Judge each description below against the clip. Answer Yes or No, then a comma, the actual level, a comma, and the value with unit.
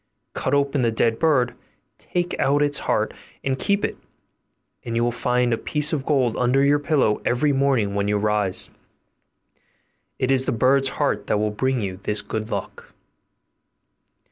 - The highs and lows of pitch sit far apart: No, average, 4.2 semitones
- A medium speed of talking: Yes, average, 170 wpm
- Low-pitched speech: Yes, low, 125 Hz